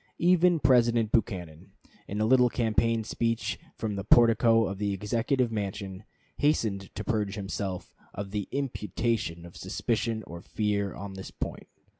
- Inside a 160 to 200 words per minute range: No, average, 145 wpm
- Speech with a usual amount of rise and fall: Yes, average, 3.0 semitones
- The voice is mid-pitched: No, low, 110 Hz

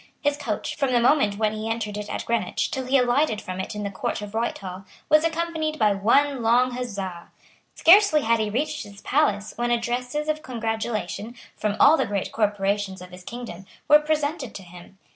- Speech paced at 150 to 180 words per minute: No, average, 195 wpm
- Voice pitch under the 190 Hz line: No, high, 230 Hz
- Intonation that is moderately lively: No, wide, 5.9 semitones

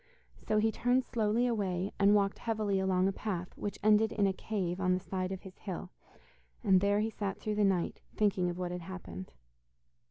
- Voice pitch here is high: Yes, high, 195 Hz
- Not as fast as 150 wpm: No, average, 200 wpm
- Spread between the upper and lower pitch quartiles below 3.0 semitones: Yes, narrow, 2.5 semitones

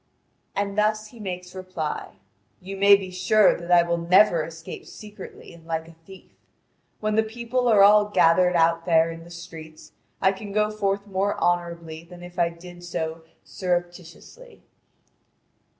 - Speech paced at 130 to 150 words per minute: No, average, 160 wpm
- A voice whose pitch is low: No, medium, 180 Hz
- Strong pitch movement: No, average, 3.3 semitones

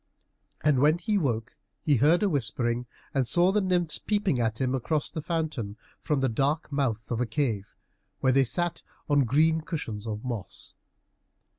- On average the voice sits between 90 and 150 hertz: Yes, medium, 140 Hz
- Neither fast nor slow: Yes, average, 170 wpm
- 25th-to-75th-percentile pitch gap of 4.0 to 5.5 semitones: Yes, average, 5.2 semitones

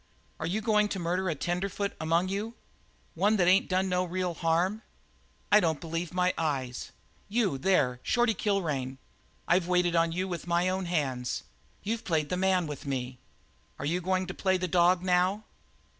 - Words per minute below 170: No, average, 175 wpm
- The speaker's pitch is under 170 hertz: No, medium, 180 Hz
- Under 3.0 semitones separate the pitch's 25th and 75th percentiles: Yes, narrow, 2.6 semitones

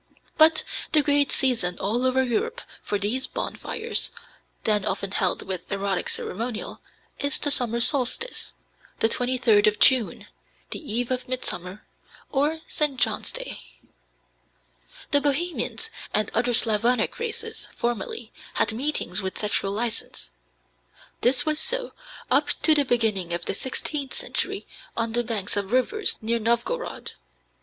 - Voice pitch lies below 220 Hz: No, high, 245 Hz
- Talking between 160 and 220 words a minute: No, slow, 135 wpm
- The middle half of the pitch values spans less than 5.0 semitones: No, wide, 5.4 semitones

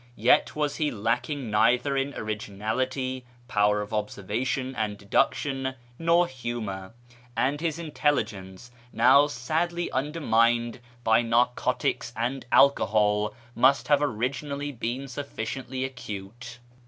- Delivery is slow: Yes, slow, 105 wpm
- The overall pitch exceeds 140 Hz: No, low, 125 Hz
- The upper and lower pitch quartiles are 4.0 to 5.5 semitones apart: Yes, average, 4.4 semitones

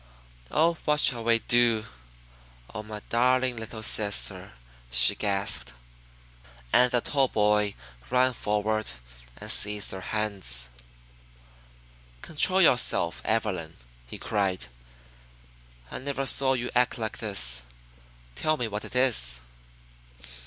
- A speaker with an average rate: No, slow, 115 wpm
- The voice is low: Yes, low, 110 Hz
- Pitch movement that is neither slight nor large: Yes, average, 3.7 semitones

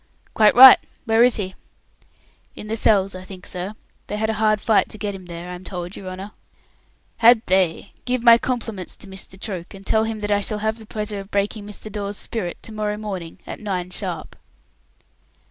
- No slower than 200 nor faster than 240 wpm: Yes, fast, 205 wpm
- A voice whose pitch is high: Yes, high, 205 Hz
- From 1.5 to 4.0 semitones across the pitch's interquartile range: Yes, narrow, 2.6 semitones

